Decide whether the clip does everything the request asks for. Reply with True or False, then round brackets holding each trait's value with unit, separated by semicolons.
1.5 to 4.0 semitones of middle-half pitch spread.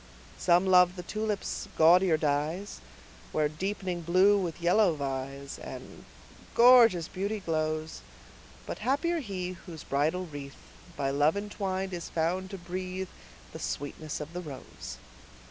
True (3.7 semitones)